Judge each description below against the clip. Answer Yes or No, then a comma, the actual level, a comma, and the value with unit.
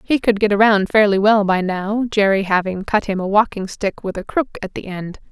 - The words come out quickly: Yes, fast, 235 wpm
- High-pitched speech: Yes, high, 200 Hz